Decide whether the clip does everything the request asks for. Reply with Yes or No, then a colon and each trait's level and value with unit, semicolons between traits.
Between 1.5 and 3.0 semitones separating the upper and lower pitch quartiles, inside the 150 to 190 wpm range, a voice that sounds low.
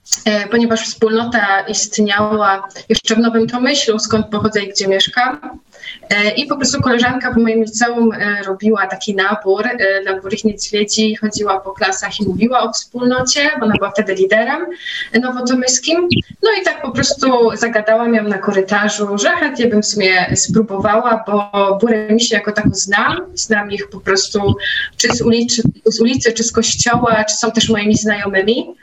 No: average, 2.7 semitones; fast, 160 wpm; high, 220 Hz